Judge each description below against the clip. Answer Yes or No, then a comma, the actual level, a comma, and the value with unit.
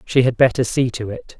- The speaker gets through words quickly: Yes, fast, 260 wpm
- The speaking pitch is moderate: No, low, 120 Hz